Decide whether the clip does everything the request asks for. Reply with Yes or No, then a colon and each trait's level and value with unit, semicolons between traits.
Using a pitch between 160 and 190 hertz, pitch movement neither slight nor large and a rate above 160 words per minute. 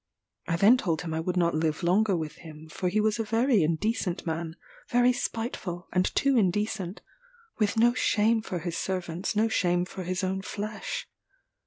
Yes: medium, 185 Hz; average, 4.2 semitones; average, 180 wpm